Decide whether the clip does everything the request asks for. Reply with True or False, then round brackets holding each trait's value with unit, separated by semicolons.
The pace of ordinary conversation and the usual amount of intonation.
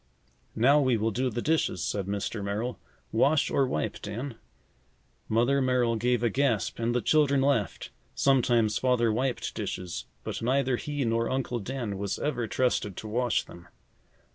True (160 wpm; 3.4 semitones)